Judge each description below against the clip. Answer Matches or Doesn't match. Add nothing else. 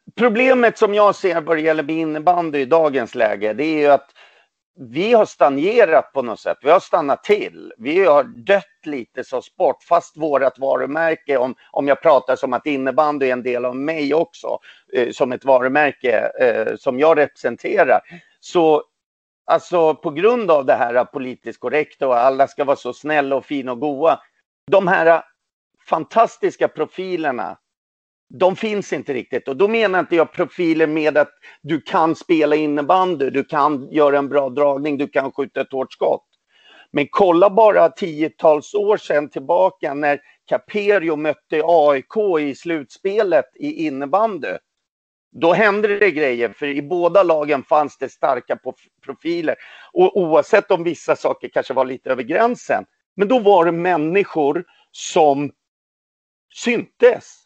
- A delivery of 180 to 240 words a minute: Doesn't match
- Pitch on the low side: Doesn't match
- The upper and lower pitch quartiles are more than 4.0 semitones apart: Matches